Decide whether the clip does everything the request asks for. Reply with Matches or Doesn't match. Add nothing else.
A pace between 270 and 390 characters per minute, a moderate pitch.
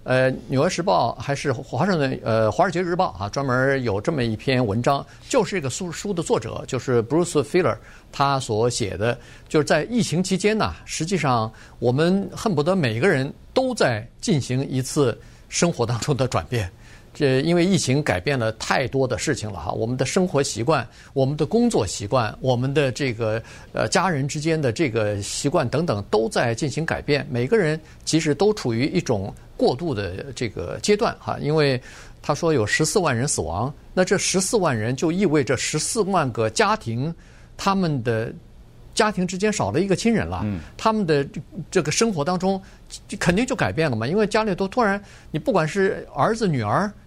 Matches